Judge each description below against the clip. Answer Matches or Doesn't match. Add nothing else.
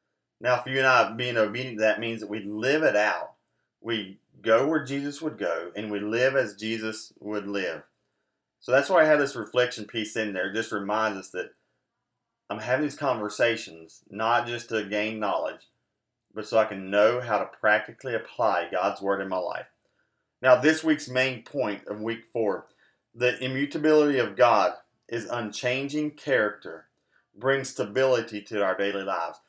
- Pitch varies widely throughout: Doesn't match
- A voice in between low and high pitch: Doesn't match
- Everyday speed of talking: Matches